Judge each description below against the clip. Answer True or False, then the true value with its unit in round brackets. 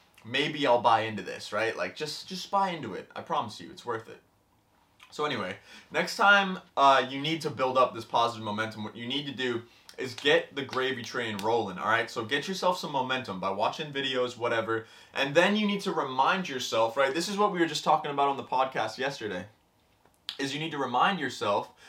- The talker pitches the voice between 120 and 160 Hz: True (140 Hz)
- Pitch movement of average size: False (5.8 semitones)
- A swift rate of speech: True (215 wpm)